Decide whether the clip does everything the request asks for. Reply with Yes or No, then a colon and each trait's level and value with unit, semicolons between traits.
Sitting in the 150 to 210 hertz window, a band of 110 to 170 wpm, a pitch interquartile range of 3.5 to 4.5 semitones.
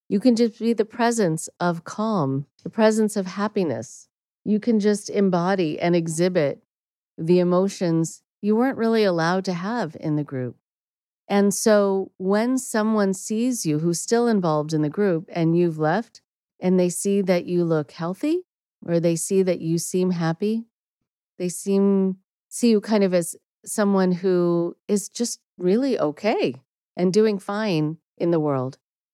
Yes: high, 190 Hz; average, 160 wpm; average, 4.1 semitones